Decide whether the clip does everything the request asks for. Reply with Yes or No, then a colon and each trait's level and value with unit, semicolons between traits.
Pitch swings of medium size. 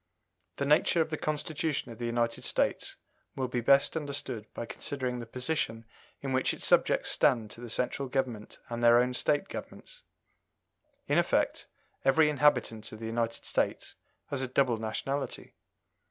Yes: average, 3.2 semitones